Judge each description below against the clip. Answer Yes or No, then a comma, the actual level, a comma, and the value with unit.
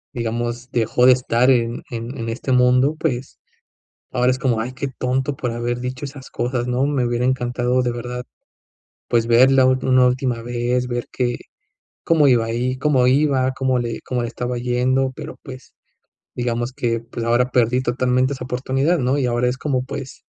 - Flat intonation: Yes, narrow, 1.3 semitones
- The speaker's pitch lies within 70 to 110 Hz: No, low, 125 Hz